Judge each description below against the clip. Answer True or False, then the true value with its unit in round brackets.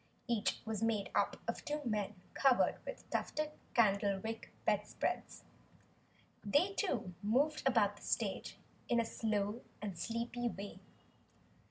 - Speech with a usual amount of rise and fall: True (3.2 semitones)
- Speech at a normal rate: False (125 wpm)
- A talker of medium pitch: False (225 Hz)